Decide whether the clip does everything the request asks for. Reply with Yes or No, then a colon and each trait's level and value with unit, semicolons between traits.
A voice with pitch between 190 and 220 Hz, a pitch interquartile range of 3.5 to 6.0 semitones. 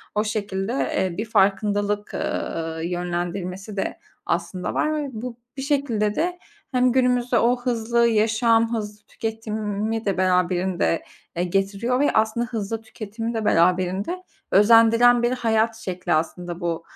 Yes: high, 215 Hz; average, 3.8 semitones